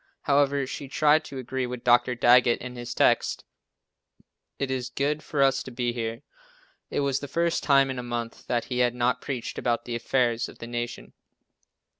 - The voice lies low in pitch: Yes, low, 125 Hz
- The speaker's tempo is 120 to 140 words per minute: No, average, 190 wpm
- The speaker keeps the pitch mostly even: Yes, narrow, 2.3 semitones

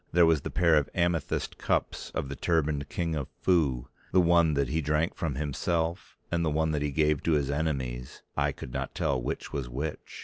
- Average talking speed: No, fast, 210 wpm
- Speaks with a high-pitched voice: No, very low, 75 Hz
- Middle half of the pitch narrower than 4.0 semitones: Yes, average, 2.9 semitones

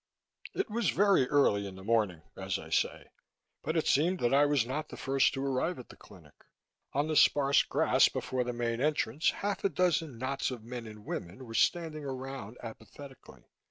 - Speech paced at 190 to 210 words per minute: Yes, average, 195 wpm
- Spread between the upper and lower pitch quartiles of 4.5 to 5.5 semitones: Yes, average, 4.8 semitones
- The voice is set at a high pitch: No, low, 135 Hz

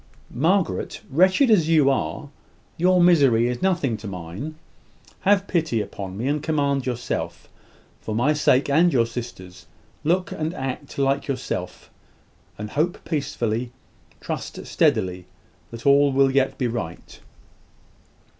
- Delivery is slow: Yes, slow, 130 wpm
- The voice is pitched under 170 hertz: Yes, medium, 140 Hz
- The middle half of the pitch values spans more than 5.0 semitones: Yes, wide, 5.4 semitones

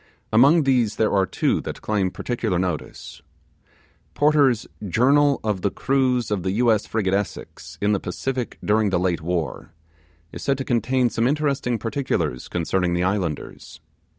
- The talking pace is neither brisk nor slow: Yes, average, 150 wpm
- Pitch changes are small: No, wide, 5.6 semitones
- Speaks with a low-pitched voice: Yes, low, 110 Hz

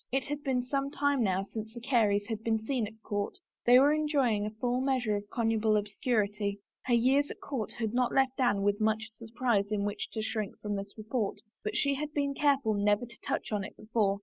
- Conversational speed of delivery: No, fast, 220 wpm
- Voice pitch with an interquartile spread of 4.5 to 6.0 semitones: No, average, 3.9 semitones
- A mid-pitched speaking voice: No, high, 225 Hz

